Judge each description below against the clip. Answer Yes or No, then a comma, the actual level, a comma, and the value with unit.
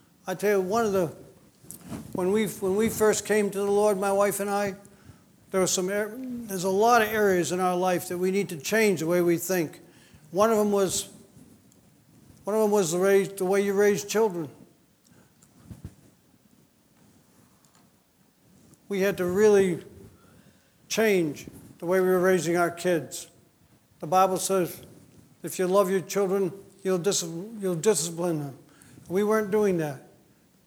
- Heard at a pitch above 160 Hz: Yes, high, 190 Hz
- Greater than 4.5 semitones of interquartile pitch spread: No, narrow, 2.4 semitones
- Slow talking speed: No, average, 160 wpm